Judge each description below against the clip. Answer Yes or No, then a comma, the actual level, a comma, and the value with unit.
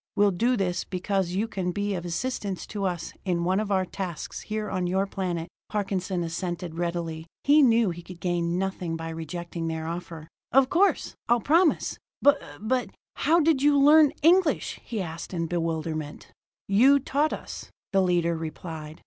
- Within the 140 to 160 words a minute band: No, average, 170 wpm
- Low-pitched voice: No, medium, 185 Hz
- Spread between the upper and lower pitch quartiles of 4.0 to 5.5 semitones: Yes, average, 5.0 semitones